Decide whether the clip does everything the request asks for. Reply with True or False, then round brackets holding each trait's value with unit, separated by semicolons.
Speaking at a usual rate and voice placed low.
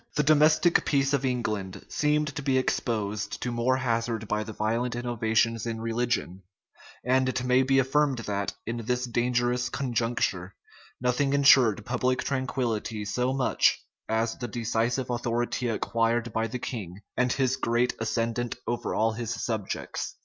True (150 wpm; 120 Hz)